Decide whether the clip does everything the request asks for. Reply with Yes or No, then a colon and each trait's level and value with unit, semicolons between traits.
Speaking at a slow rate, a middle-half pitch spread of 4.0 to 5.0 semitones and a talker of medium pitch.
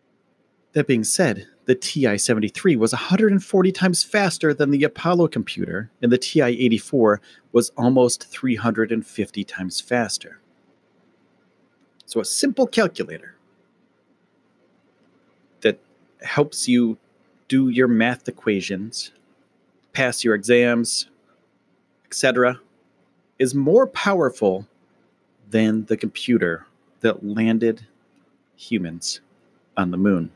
No: slow, 95 wpm; average, 4.5 semitones; low, 120 Hz